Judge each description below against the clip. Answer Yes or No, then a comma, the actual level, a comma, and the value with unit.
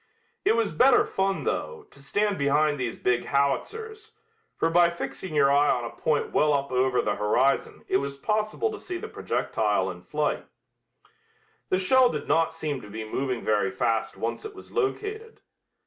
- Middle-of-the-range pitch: Yes, medium, 155 Hz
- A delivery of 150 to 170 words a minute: No, average, 180 wpm